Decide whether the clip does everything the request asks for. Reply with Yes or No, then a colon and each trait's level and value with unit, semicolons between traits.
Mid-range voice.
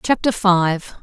No: high, 195 Hz